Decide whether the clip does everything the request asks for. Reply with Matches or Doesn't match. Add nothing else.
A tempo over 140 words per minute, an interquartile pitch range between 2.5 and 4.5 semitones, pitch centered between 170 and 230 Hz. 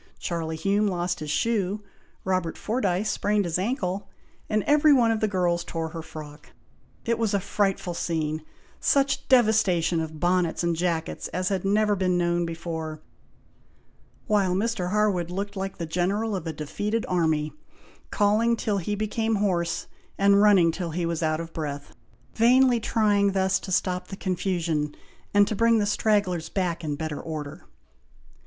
Matches